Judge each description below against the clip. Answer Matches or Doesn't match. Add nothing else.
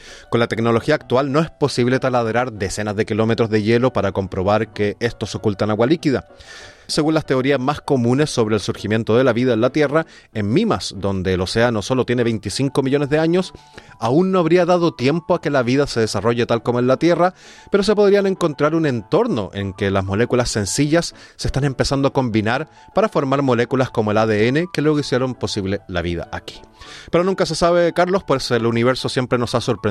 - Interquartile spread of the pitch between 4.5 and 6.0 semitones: Matches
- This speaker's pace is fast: Matches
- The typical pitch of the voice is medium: Doesn't match